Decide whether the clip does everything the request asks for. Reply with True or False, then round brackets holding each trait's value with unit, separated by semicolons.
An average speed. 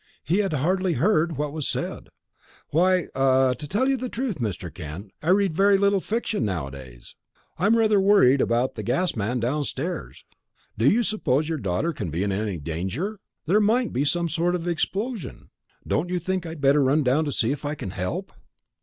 True (195 wpm)